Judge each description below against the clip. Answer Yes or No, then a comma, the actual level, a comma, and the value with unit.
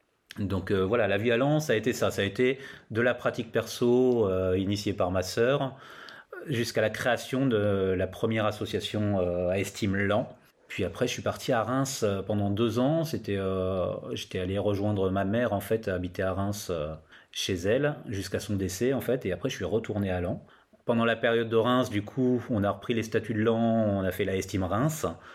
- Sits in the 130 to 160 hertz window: No, low, 105 Hz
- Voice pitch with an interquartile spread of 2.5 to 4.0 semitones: Yes, average, 3.7 semitones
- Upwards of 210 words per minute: Yes, fast, 220 wpm